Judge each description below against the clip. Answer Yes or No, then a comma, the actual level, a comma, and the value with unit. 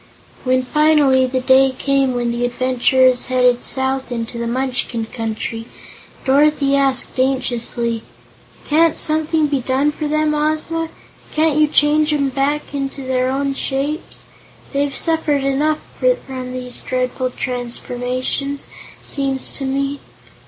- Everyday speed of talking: No, slow, 125 wpm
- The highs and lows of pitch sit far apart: No, average, 2.7 semitones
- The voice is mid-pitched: No, very high, 270 Hz